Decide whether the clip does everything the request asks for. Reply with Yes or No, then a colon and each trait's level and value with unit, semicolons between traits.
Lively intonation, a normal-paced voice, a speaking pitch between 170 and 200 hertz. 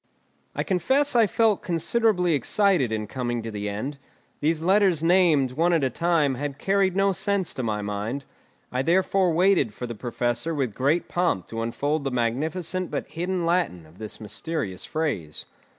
No: wide, 7.1 semitones; average, 170 wpm; medium, 155 Hz